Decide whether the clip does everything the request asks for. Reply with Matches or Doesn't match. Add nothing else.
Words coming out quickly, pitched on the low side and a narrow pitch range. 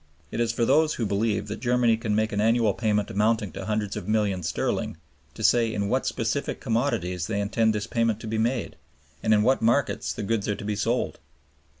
Matches